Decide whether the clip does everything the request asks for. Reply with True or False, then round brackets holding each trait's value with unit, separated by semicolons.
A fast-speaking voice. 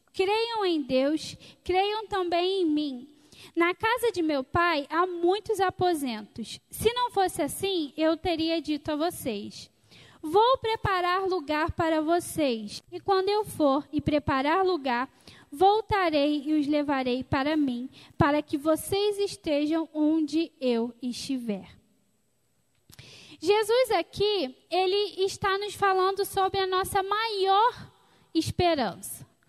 False (120 wpm)